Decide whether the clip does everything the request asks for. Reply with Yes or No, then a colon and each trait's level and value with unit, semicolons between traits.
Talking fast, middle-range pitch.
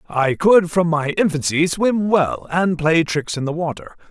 No: average, 190 wpm; medium, 165 Hz